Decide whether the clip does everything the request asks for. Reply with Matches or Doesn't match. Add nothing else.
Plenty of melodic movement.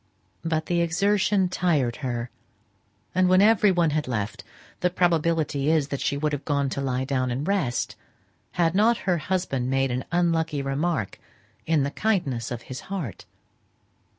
Doesn't match